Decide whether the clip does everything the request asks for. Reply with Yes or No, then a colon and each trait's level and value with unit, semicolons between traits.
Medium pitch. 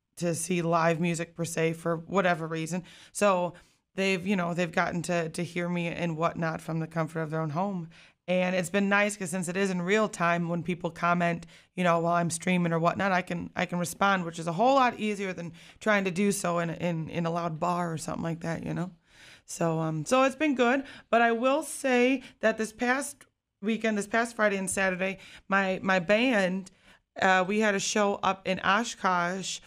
Yes: medium, 180 Hz